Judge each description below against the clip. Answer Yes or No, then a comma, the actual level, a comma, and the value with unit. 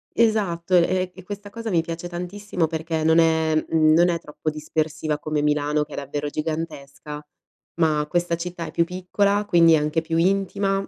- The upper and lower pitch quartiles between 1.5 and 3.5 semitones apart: Yes, average, 2.8 semitones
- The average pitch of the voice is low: No, medium, 165 Hz